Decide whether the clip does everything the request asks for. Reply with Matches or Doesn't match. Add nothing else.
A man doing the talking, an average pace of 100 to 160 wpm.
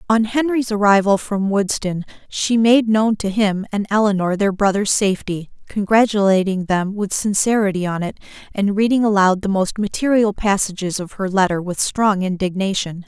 Doesn't match